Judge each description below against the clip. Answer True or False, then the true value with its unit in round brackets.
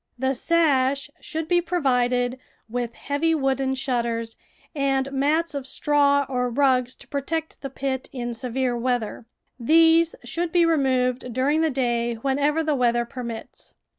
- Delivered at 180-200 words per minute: False (140 wpm)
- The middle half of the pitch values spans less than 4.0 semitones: True (3.1 semitones)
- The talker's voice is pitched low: False (265 Hz)